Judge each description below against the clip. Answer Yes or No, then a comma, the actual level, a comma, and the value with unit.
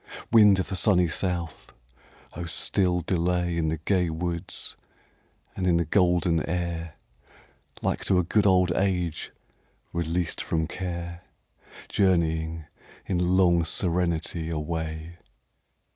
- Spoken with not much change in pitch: Yes, narrow, 1.7 semitones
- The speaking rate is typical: No, slow, 115 wpm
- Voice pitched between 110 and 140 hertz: No, very low, 85 Hz